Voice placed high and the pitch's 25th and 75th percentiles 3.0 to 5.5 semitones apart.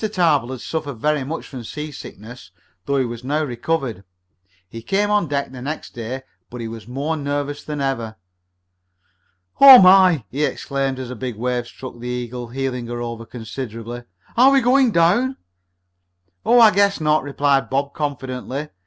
No: low, 135 Hz; average, 4.3 semitones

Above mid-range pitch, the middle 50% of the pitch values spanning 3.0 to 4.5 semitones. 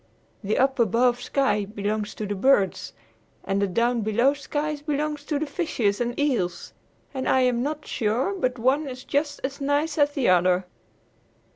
No: very high, 255 Hz; average, 5.2 semitones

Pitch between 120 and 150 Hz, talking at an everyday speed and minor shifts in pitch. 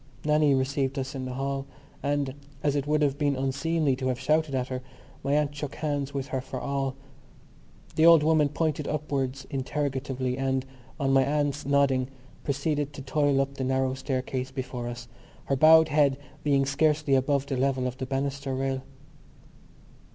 Yes: medium, 140 Hz; average, 175 wpm; narrow, 1.7 semitones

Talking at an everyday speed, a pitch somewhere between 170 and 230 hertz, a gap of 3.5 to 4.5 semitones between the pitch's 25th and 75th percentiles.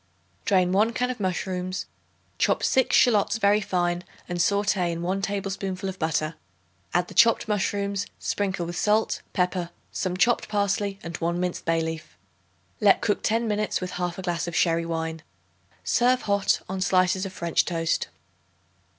No: average, 160 wpm; medium, 185 Hz; average, 2.8 semitones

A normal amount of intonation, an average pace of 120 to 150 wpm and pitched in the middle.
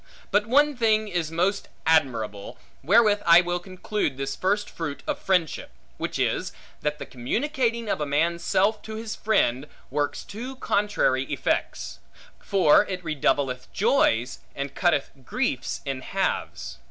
No: wide, 7.2 semitones; average, 140 wpm; medium, 180 Hz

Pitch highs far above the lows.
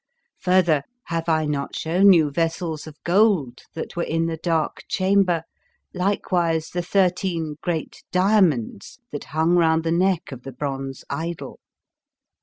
No: average, 2.7 semitones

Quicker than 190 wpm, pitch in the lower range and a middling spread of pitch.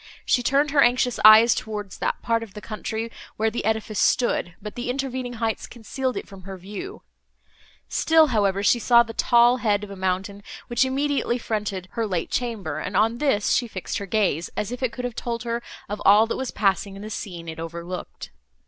No: fast, 205 wpm; high, 220 Hz; average, 3.5 semitones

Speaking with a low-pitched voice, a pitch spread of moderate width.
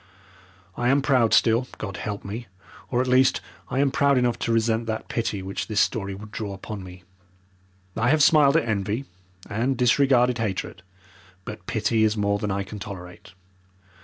Yes: low, 115 Hz; average, 3.7 semitones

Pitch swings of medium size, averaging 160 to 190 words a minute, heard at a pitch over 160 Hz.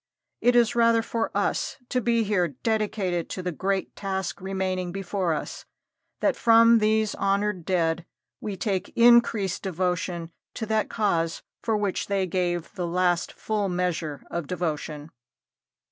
No: average, 3.6 semitones; average, 145 wpm; high, 190 Hz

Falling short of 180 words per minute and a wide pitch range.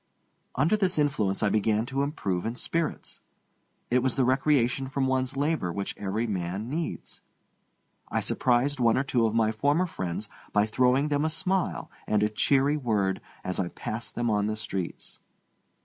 No: average, 170 wpm; average, 5.0 semitones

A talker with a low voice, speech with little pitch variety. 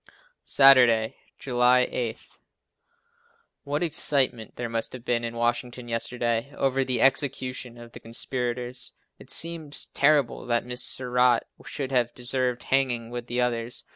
Yes: low, 125 Hz; narrow, 1.9 semitones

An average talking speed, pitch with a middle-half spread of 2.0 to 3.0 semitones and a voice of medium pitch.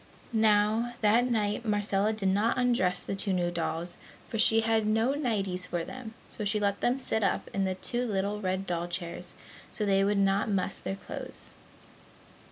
No: average, 180 wpm; average, 2.7 semitones; high, 205 Hz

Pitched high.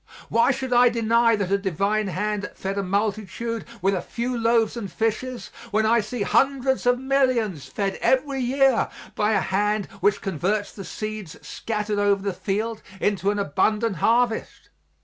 Yes: high, 215 Hz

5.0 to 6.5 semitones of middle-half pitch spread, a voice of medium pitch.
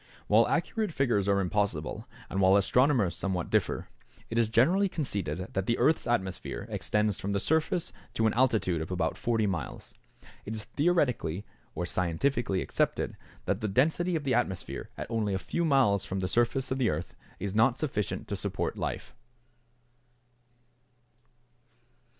No: wide, 5.6 semitones; low, 105 Hz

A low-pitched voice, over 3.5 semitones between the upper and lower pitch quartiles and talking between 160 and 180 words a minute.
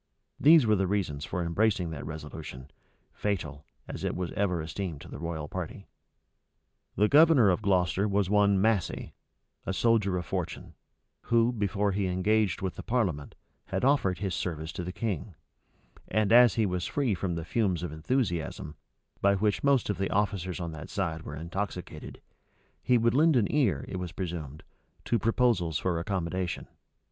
Yes: very low, 95 Hz; average, 4.2 semitones; average, 170 wpm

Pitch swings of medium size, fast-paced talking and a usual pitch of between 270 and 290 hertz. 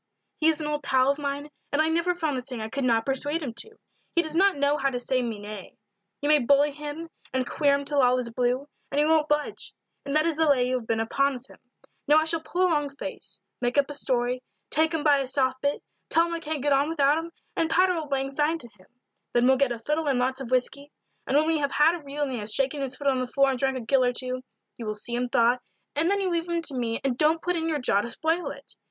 Yes: average, 3.5 semitones; fast, 285 wpm; very high, 280 Hz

